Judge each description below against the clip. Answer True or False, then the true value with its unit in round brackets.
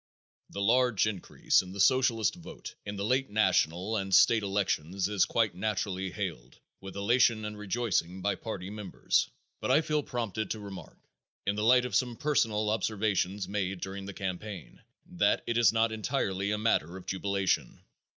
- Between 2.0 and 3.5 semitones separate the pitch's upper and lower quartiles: True (2.9 semitones)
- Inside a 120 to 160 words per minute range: False (170 wpm)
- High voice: False (105 Hz)